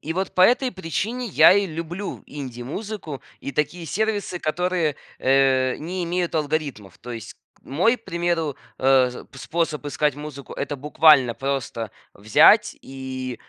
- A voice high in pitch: No, medium, 150 Hz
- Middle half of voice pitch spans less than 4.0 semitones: No, average, 5.1 semitones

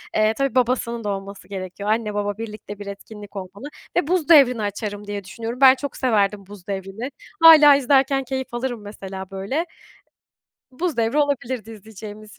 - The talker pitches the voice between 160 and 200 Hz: No, high, 220 Hz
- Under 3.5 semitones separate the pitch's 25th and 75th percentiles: No, average, 4.5 semitones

